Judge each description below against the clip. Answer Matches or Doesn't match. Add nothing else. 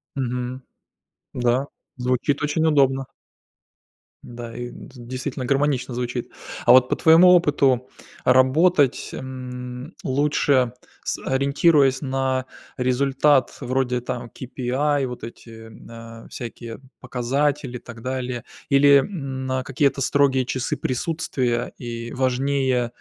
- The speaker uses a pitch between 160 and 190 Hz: Doesn't match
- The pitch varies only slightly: Matches